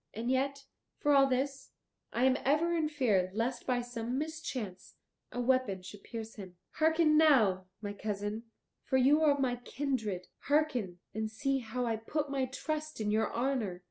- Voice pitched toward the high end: Yes, very high, 250 Hz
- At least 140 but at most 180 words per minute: Yes, average, 175 wpm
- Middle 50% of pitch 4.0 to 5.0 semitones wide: Yes, average, 4.5 semitones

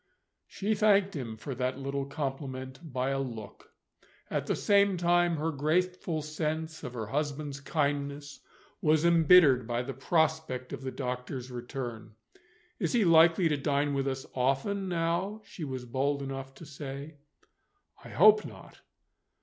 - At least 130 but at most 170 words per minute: Yes, average, 150 wpm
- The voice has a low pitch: No, medium, 145 Hz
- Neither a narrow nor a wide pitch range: Yes, average, 3.9 semitones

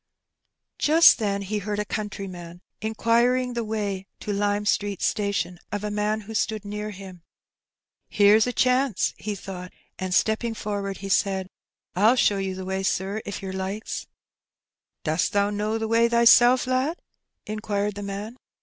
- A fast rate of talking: No, average, 160 wpm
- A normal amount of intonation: No, narrow, 2.0 semitones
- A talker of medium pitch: No, high, 205 Hz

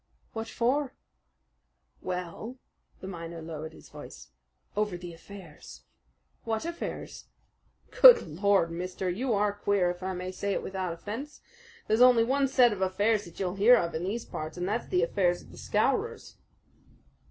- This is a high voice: Yes, high, 195 Hz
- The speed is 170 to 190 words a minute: No, average, 160 wpm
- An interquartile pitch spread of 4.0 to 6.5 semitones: Yes, average, 4.3 semitones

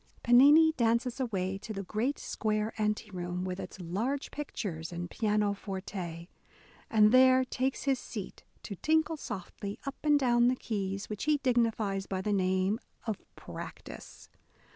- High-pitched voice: Yes, high, 215 Hz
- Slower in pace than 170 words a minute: Yes, average, 145 wpm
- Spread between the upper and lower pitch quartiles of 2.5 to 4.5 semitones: No, average, 4.9 semitones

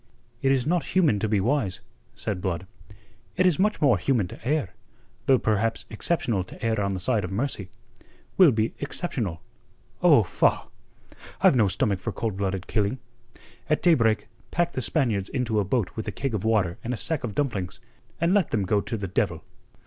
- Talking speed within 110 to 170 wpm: No, average, 190 wpm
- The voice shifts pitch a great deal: Yes, wide, 5.7 semitones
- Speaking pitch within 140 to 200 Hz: No, low, 110 Hz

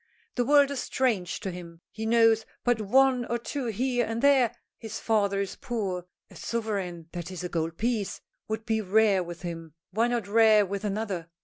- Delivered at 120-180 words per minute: No, average, 190 wpm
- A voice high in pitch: Yes, high, 220 Hz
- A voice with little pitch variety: No, average, 4.3 semitones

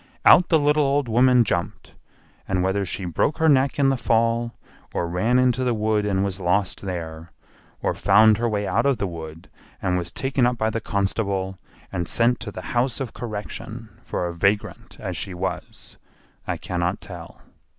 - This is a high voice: No, low, 105 Hz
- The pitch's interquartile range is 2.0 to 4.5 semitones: No, average, 4.9 semitones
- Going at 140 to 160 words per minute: No, average, 185 wpm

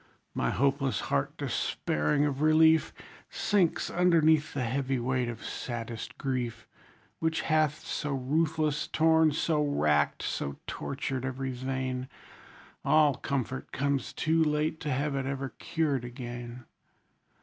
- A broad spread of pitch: No, average, 3.4 semitones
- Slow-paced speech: Yes, slow, 125 wpm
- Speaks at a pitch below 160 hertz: Yes, medium, 140 Hz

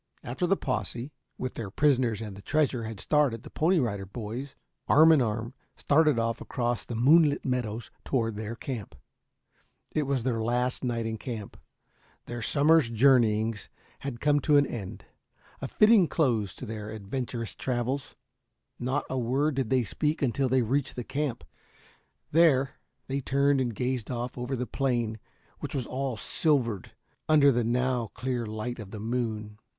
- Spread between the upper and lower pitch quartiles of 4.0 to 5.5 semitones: No, average, 3.5 semitones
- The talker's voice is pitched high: No, low, 125 Hz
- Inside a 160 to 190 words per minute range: Yes, average, 165 wpm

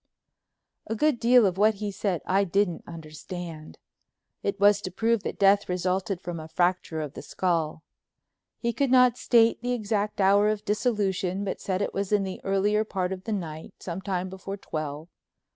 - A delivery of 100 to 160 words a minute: No, average, 175 wpm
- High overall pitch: Yes, high, 195 Hz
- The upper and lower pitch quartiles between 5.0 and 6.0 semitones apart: No, average, 2.9 semitones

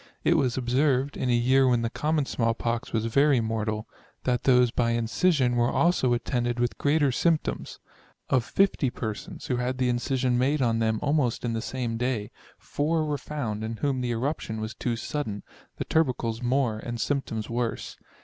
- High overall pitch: No, low, 125 Hz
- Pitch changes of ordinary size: Yes, average, 3.0 semitones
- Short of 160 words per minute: No, average, 185 wpm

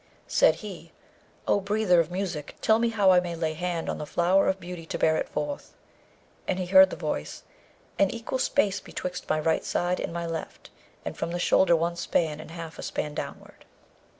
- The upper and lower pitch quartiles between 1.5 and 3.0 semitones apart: Yes, narrow, 2.6 semitones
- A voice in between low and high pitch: Yes, medium, 175 Hz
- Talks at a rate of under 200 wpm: No, fast, 205 wpm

